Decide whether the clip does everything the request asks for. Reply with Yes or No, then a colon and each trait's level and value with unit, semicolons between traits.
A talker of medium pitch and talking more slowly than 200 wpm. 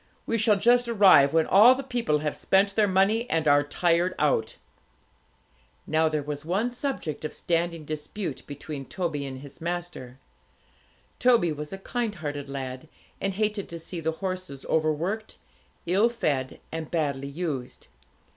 Yes: medium, 165 Hz; average, 155 wpm